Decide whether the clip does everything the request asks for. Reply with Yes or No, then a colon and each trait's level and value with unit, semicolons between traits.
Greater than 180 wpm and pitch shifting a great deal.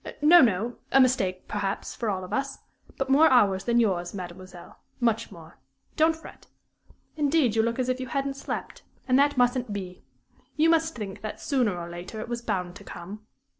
Yes: average, 190 wpm; wide, 6.0 semitones